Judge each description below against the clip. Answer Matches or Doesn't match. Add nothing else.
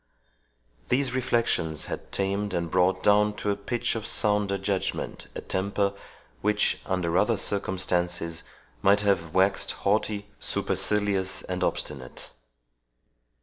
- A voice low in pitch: Matches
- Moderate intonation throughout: Doesn't match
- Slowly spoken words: Matches